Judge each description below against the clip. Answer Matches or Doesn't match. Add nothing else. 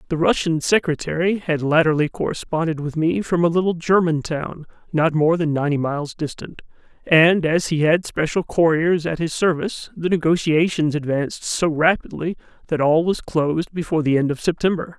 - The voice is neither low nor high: Matches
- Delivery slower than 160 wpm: Doesn't match